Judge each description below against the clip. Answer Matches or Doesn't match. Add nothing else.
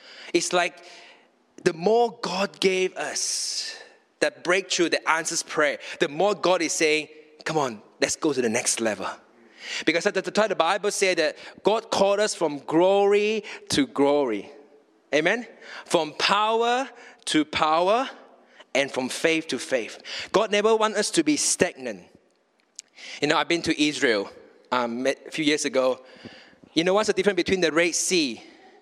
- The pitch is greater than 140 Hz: Matches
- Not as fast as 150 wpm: Doesn't match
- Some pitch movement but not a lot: Doesn't match